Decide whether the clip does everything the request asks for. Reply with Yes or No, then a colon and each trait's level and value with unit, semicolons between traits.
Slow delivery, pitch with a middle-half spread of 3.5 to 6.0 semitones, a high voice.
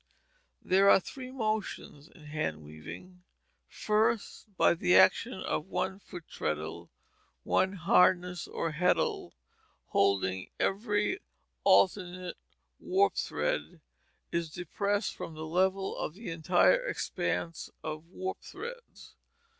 No: slow, 110 wpm; average, 4.5 semitones; medium, 180 Hz